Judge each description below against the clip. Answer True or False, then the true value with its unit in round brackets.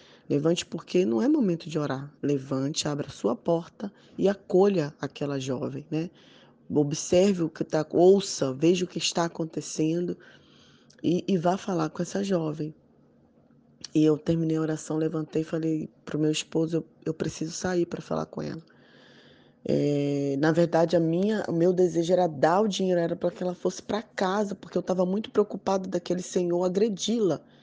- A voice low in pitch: False (170 Hz)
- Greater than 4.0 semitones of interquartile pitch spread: False (2.9 semitones)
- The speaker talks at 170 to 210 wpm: True (175 wpm)